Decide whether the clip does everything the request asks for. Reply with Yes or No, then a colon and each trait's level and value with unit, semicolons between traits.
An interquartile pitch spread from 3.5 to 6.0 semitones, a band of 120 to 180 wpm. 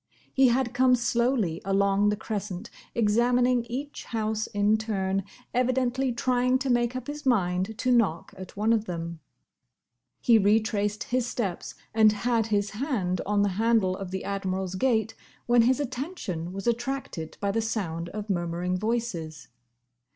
Yes: average, 4.0 semitones; average, 150 wpm